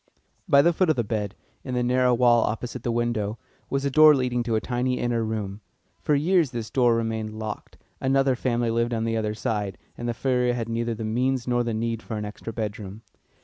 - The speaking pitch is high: No, low, 120 Hz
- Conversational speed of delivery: No, fast, 220 wpm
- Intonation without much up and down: Yes, narrow, 2.2 semitones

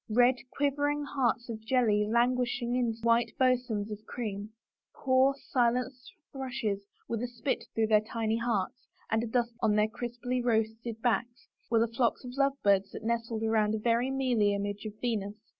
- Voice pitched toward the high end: Yes, high, 235 Hz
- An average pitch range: No, narrow, 2.3 semitones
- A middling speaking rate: Yes, average, 175 wpm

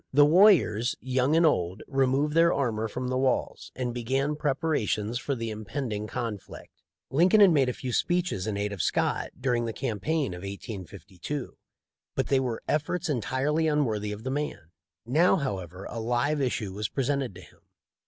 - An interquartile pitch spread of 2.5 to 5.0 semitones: No, wide, 5.4 semitones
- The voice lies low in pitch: Yes, low, 130 Hz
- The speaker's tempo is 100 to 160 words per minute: No, average, 170 wpm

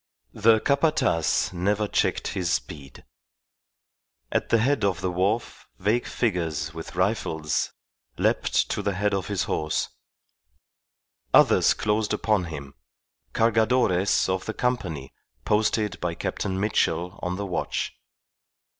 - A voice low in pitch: Yes, low, 100 Hz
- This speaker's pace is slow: Yes, slow, 120 wpm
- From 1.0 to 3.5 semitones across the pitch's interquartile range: No, average, 3.9 semitones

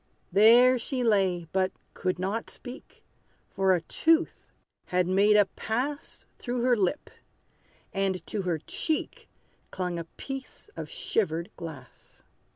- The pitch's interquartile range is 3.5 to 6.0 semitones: Yes, average, 5.3 semitones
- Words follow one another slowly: Yes, slow, 130 wpm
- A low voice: No, high, 200 Hz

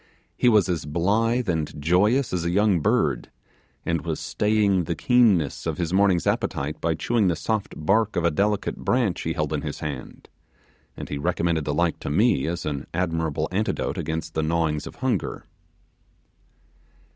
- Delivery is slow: No, average, 170 wpm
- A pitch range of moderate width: Yes, average, 4.6 semitones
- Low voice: Yes, very low, 85 Hz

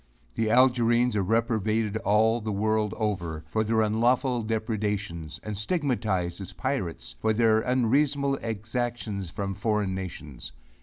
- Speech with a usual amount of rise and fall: Yes, average, 3.1 semitones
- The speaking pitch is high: No, low, 110 Hz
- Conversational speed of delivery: No, slow, 125 wpm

